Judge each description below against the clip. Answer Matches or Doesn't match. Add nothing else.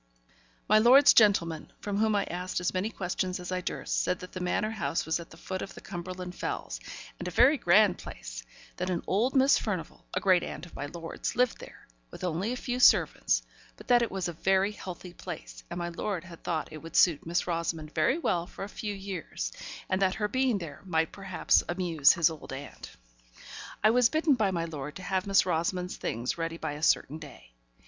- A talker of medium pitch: Matches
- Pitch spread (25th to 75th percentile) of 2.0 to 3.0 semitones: Doesn't match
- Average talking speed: Doesn't match